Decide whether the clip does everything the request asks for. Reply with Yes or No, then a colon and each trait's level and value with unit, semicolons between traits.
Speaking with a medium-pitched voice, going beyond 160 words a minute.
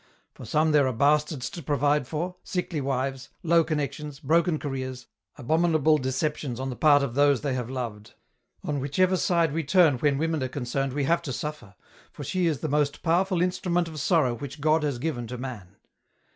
Yes: medium, 145 Hz; average, 190 wpm